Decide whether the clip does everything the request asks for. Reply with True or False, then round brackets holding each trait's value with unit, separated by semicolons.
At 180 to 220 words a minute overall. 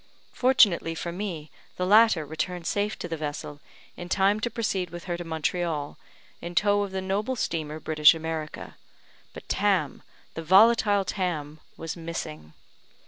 False (150 wpm)